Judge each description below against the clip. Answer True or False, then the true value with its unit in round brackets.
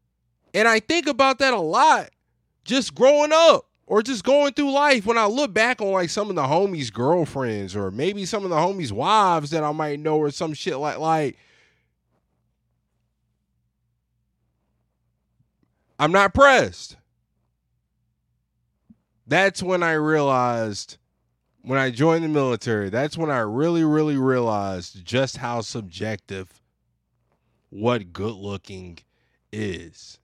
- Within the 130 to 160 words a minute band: True (135 wpm)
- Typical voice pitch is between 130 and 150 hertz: True (140 Hz)